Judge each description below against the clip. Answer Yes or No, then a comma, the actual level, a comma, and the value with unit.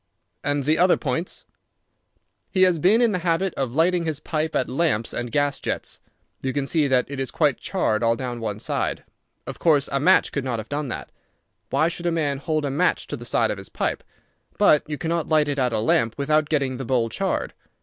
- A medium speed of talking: No, fast, 220 wpm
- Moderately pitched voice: Yes, medium, 145 Hz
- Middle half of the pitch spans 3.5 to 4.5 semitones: Yes, average, 3.9 semitones